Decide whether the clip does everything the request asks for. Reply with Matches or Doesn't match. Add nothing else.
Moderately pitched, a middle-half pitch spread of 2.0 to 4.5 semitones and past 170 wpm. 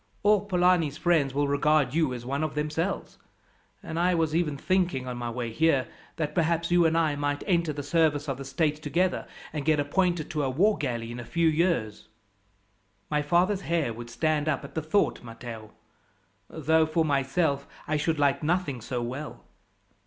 Matches